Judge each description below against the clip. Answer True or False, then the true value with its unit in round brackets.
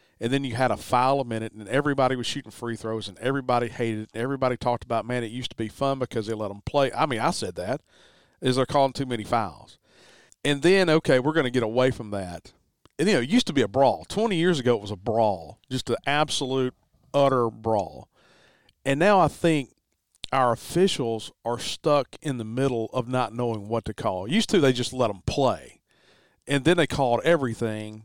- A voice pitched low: True (125 Hz)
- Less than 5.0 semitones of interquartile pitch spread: True (3.4 semitones)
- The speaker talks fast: True (220 wpm)